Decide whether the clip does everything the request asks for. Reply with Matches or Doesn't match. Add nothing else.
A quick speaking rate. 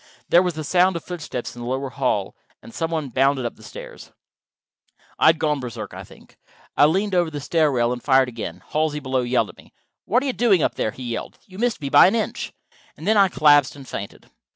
Matches